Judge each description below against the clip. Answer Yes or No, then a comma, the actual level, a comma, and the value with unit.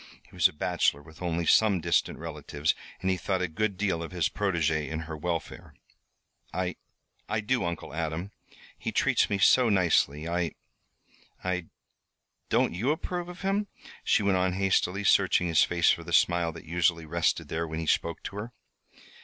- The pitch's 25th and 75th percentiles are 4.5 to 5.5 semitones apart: No, average, 3.2 semitones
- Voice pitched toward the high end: No, very low, 90 Hz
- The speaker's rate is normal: Yes, average, 180 wpm